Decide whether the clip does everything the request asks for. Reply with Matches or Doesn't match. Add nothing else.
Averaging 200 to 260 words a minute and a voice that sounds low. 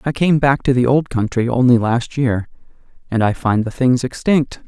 Matches